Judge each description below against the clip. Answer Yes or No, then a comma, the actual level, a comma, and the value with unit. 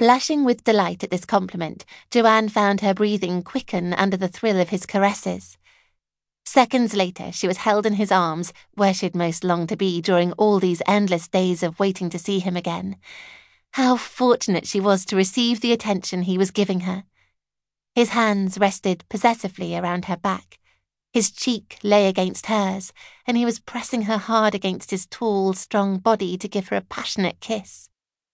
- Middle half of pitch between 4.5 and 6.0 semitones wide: No, average, 3.2 semitones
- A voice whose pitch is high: Yes, high, 195 Hz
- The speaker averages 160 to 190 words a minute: Yes, average, 175 wpm